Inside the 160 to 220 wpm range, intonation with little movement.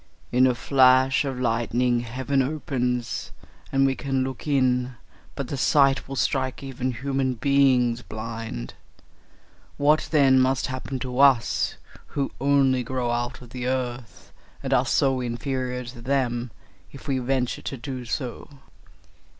No: average, 140 wpm; narrow, 1.7 semitones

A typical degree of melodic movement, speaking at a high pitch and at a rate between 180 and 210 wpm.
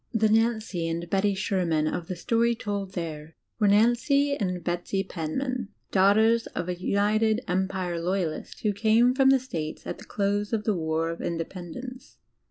No: average, 4.5 semitones; high, 200 Hz; average, 170 wpm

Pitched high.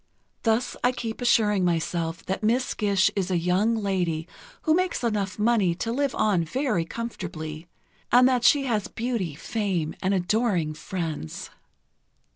Yes: high, 205 Hz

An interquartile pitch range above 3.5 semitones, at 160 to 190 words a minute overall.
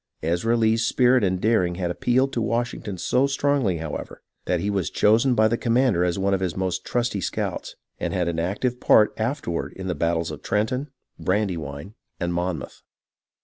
Yes: average, 5.2 semitones; average, 180 wpm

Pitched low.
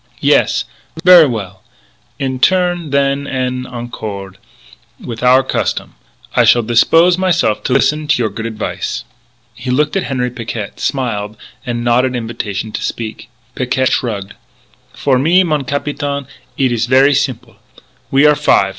Yes: low, 125 Hz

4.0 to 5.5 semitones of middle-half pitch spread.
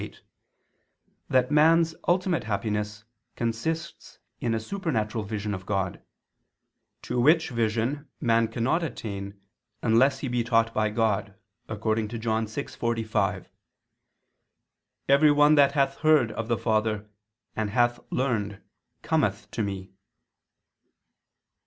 Yes: average, 4.3 semitones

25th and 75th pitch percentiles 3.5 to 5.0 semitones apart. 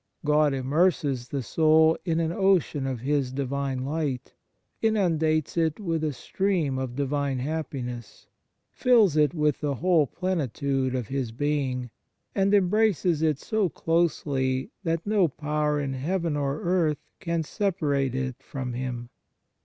Yes: average, 4.1 semitones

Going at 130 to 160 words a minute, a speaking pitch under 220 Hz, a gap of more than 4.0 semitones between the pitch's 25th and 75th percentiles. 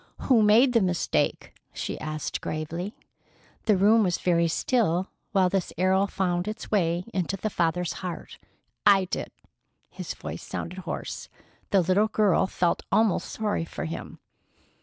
No: average, 145 wpm; medium, 185 Hz; average, 3.1 semitones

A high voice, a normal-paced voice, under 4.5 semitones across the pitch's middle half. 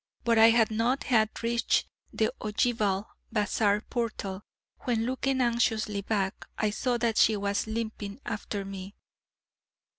No: high, 220 Hz; slow, 130 wpm; narrow, 2.4 semitones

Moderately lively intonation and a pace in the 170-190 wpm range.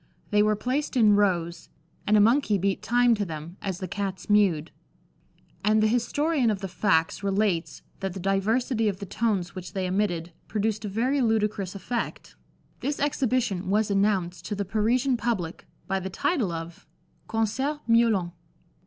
No: average, 3.5 semitones; average, 160 wpm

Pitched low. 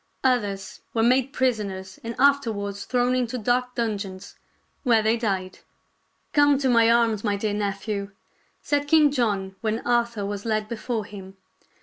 No: high, 225 Hz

